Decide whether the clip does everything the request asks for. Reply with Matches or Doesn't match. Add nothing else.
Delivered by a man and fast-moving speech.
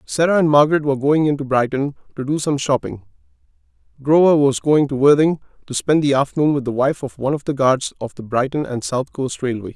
Matches